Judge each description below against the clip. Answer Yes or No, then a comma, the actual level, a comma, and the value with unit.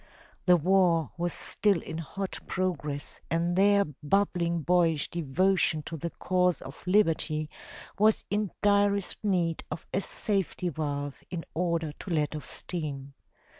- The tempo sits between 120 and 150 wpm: Yes, slow, 135 wpm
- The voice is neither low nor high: Yes, medium, 170 Hz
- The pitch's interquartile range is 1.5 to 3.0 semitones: No, average, 3.6 semitones